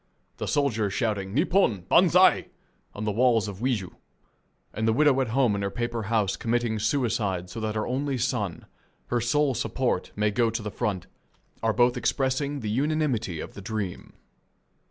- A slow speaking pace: No, average, 165 wpm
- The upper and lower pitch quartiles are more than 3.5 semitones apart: Yes, average, 3.9 semitones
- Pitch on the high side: No, low, 115 Hz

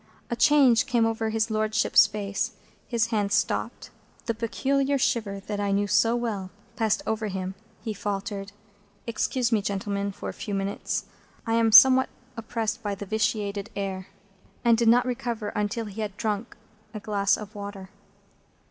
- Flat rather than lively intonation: Yes, narrow, 2.3 semitones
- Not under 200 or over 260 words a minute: No, average, 160 wpm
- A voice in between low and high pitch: No, high, 215 Hz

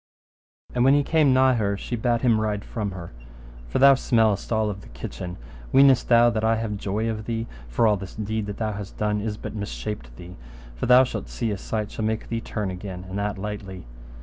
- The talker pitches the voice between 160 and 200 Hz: No, low, 110 Hz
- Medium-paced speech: No, fast, 225 wpm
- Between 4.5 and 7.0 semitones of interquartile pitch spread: No, narrow, 2.5 semitones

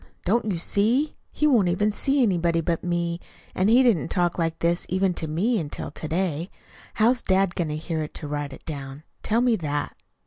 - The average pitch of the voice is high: No, medium, 175 Hz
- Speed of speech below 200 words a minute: No, fast, 205 wpm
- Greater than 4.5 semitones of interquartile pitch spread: Yes, average, 4.9 semitones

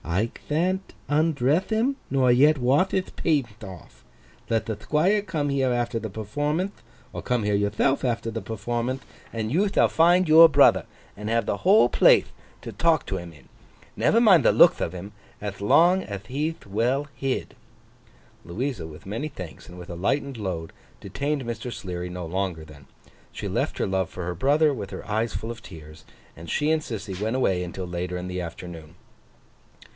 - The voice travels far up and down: Yes, wide, 7.9 semitones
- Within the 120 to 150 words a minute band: No, average, 185 wpm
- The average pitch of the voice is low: Yes, low, 115 Hz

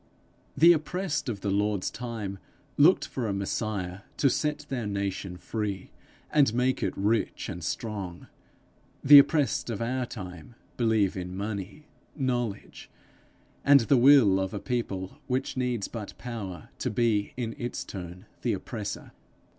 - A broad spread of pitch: No, average, 4.6 semitones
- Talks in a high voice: No, low, 110 Hz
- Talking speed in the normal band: Yes, average, 145 wpm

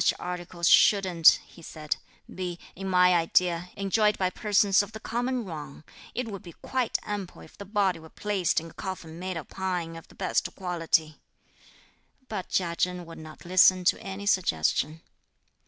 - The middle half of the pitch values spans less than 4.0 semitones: Yes, average, 2.8 semitones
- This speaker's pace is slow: No, average, 170 wpm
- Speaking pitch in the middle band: Yes, medium, 180 Hz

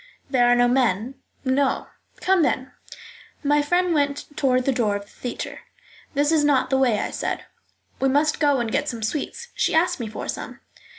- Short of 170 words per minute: No, average, 190 wpm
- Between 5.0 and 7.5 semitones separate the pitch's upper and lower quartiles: No, average, 3.3 semitones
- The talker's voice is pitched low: No, very high, 270 Hz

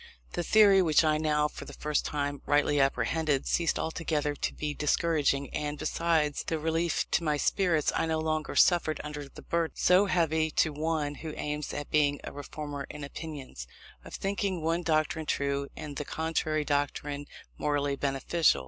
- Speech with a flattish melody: Yes, narrow, 1.9 semitones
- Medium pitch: Yes, medium, 150 Hz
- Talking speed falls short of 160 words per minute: No, average, 170 wpm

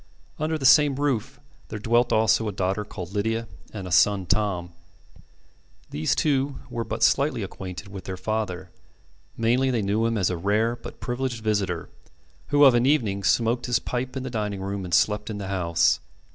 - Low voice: Yes, low, 110 Hz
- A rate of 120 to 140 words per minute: No, average, 185 wpm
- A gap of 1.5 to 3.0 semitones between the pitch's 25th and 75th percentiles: No, average, 4.0 semitones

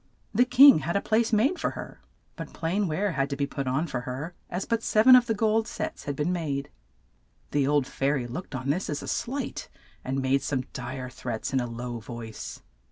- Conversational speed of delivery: No, fast, 225 wpm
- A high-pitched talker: No, medium, 145 Hz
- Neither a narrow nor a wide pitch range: No, wide, 8.0 semitones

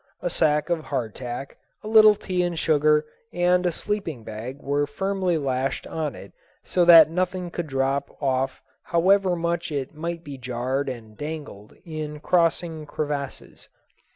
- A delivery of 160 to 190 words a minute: No, average, 150 wpm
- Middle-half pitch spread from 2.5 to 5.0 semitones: Yes, average, 4.3 semitones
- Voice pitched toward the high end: No, medium, 155 Hz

